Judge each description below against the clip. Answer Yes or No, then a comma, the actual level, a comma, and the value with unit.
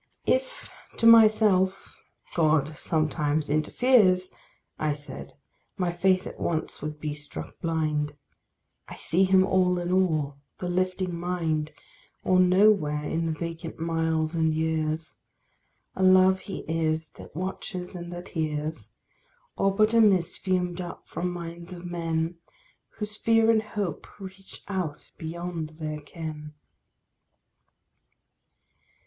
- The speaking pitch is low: No, medium, 170 Hz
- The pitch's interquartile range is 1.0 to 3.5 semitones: Yes, average, 3.1 semitones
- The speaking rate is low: Yes, slow, 125 wpm